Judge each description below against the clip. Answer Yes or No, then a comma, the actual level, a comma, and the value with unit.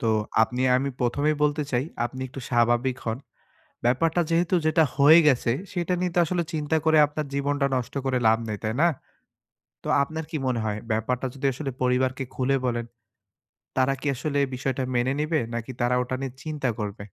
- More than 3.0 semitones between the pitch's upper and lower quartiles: Yes, average, 3.8 semitones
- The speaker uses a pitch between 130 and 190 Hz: Yes, low, 135 Hz